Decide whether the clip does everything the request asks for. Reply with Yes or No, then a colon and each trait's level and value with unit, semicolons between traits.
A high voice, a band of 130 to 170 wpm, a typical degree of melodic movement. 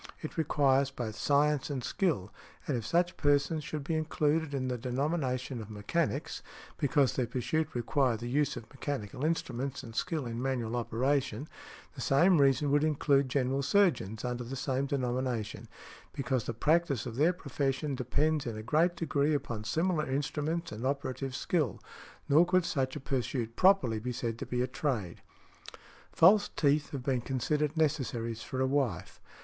No: low, 135 Hz; average, 165 wpm; average, 3.5 semitones